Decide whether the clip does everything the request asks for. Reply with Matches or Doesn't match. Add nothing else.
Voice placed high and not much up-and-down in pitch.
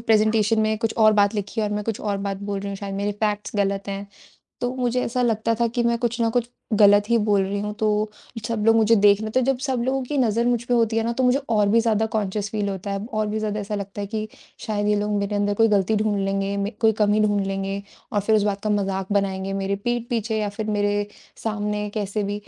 Matches